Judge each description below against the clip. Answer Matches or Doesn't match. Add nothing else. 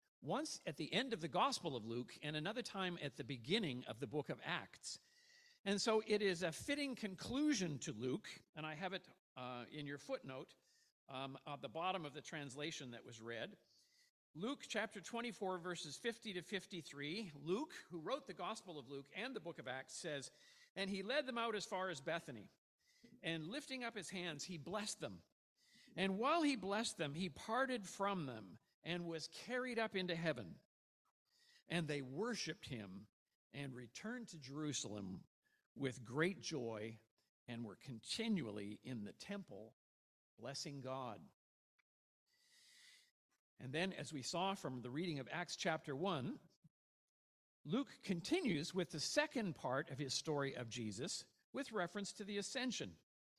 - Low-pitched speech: Doesn't match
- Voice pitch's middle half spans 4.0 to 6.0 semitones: Doesn't match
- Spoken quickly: Doesn't match